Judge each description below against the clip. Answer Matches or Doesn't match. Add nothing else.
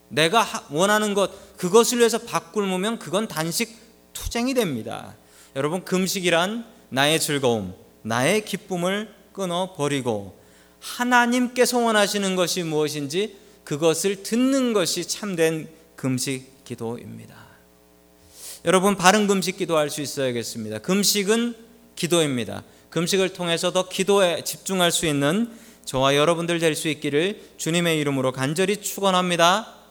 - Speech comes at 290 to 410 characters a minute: Matches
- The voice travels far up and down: Matches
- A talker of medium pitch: Matches